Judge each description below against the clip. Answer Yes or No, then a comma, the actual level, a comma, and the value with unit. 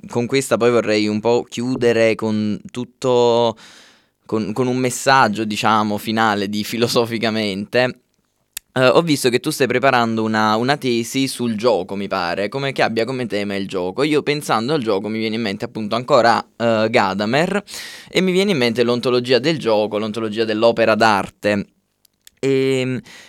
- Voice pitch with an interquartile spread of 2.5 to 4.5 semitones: Yes, average, 2.8 semitones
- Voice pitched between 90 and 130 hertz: Yes, low, 115 Hz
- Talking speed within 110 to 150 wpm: No, average, 160 wpm